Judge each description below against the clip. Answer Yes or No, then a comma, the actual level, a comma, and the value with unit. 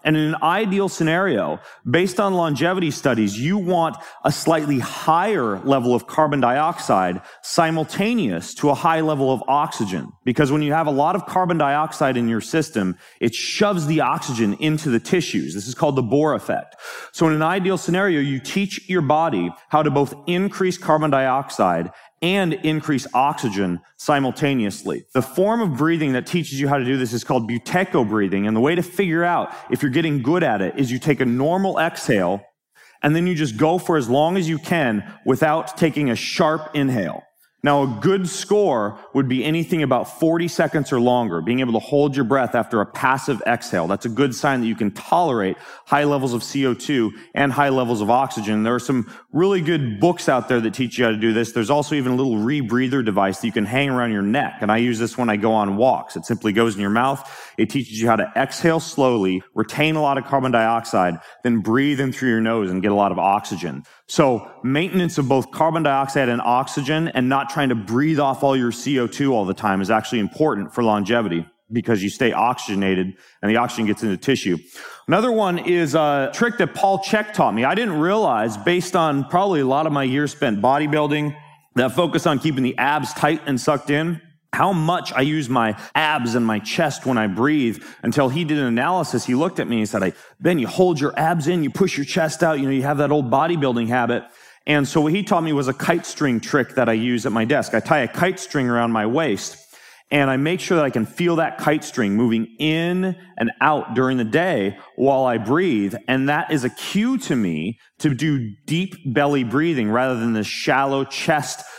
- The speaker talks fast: Yes, fast, 215 wpm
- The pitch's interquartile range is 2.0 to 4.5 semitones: No, average, 5.1 semitones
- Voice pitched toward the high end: No, medium, 140 Hz